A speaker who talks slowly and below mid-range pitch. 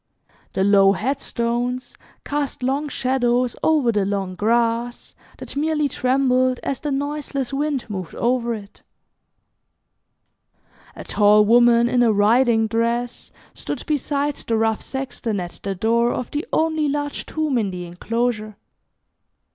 No: slow, 130 wpm; high, 240 Hz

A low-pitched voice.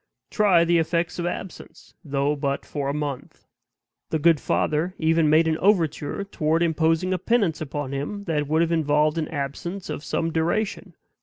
No: medium, 160 Hz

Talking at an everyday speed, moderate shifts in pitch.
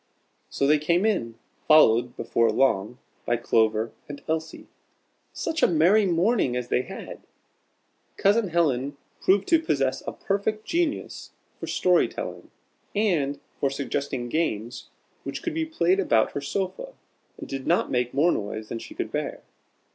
No: average, 150 wpm; wide, 8.0 semitones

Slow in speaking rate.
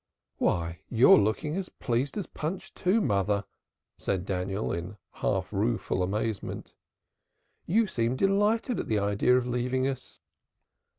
Yes: slow, 130 wpm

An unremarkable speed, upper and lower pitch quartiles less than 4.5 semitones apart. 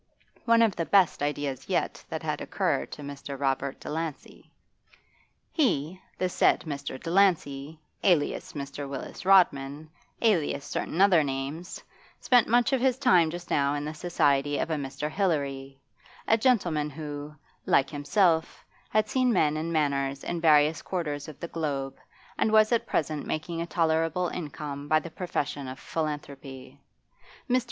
Yes: average, 150 wpm; average, 3.9 semitones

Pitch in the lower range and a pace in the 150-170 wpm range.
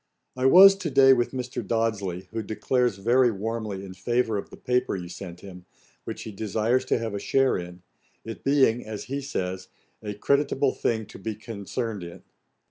No: low, 110 Hz; average, 185 wpm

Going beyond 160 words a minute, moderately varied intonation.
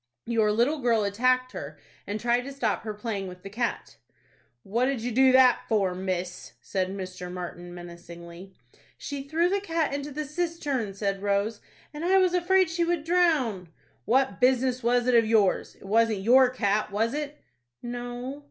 No: average, 175 wpm; wide, 5.7 semitones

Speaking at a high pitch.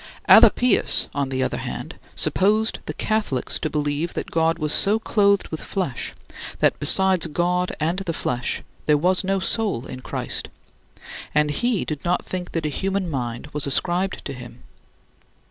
No: medium, 170 Hz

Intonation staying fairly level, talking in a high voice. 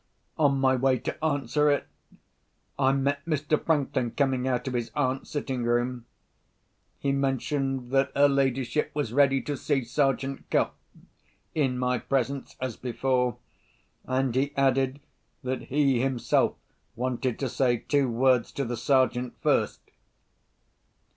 No: narrow, 1.8 semitones; low, 135 Hz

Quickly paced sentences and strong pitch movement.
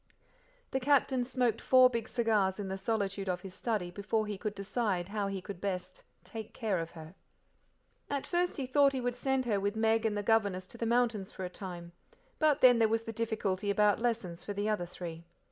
No: fast, 215 wpm; average, 3.7 semitones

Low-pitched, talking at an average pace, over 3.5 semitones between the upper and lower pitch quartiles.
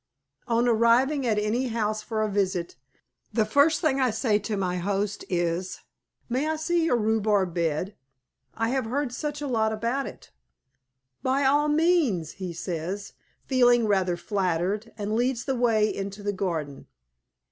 No: high, 220 Hz; average, 160 wpm; average, 4.8 semitones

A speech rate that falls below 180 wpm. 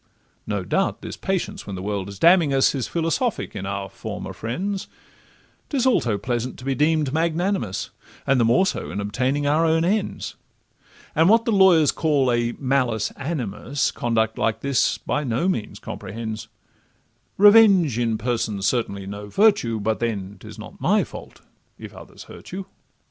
Yes: average, 165 wpm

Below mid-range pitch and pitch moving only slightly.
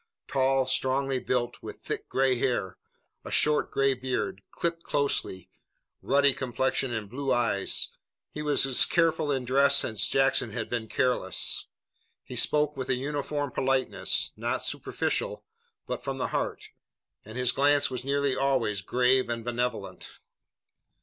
Yes: low, 130 Hz; narrow, 2.2 semitones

